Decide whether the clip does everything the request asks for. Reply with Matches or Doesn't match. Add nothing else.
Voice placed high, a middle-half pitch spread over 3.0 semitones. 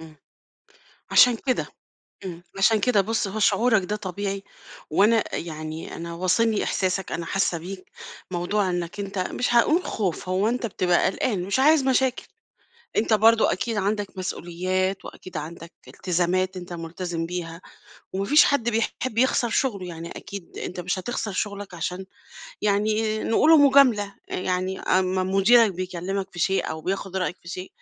Matches